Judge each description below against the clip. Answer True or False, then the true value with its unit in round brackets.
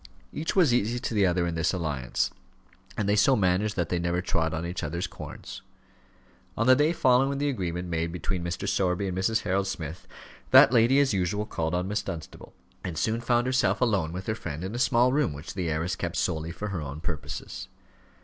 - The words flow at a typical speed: False (210 wpm)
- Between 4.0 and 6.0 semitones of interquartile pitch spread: True (5.4 semitones)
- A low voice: True (95 Hz)